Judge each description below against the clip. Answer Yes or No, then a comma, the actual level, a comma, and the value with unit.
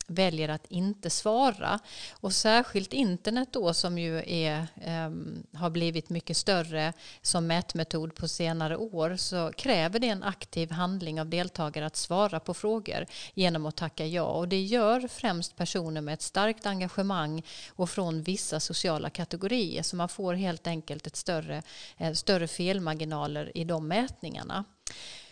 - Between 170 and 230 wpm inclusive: No, average, 150 wpm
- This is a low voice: No, medium, 170 Hz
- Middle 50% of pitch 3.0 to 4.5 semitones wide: Yes, average, 3.3 semitones